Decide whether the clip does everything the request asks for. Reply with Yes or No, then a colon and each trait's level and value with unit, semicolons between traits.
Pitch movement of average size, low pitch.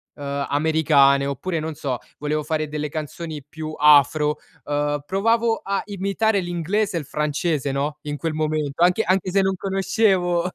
No: average, 4.2 semitones; medium, 155 Hz